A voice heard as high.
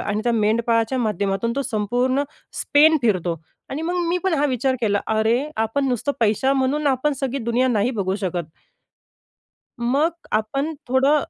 Yes: high, 245 Hz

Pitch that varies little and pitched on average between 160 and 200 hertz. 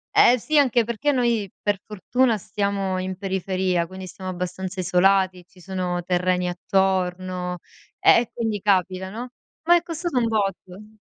No: average, 3.2 semitones; high, 190 Hz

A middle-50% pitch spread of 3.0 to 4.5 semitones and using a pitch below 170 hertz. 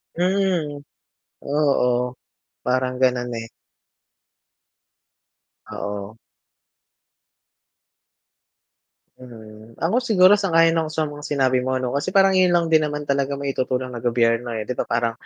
No: average, 5.0 semitones; medium, 140 Hz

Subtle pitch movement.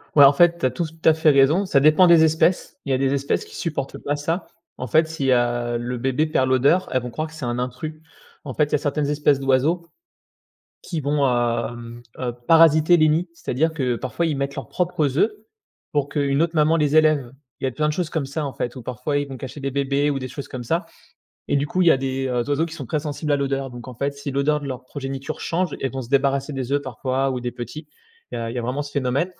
No: average, 3.2 semitones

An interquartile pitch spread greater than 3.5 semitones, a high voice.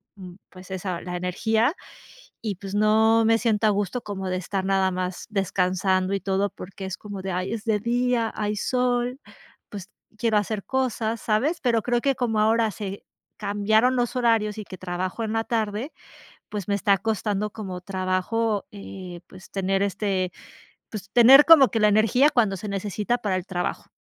No: average, 3.0 semitones; high, 210 Hz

